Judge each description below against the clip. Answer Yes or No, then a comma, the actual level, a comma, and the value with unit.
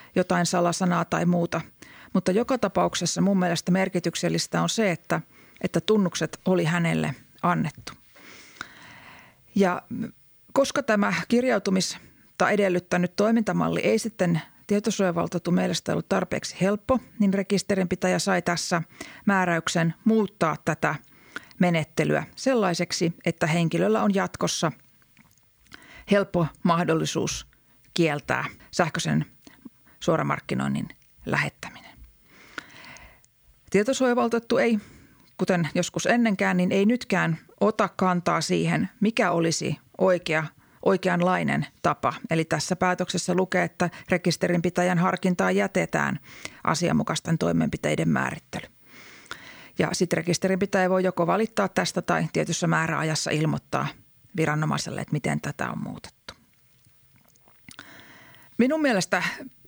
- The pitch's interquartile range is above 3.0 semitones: No, narrow, 2.6 semitones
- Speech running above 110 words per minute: No, slow, 95 wpm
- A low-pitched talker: No, medium, 180 Hz